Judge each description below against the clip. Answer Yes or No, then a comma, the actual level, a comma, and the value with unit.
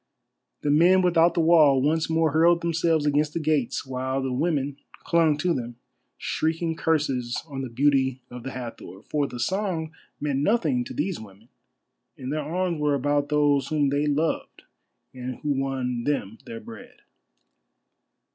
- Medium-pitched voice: Yes, medium, 145 Hz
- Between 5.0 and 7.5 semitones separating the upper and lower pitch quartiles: No, average, 3.7 semitones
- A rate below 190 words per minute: Yes, average, 160 wpm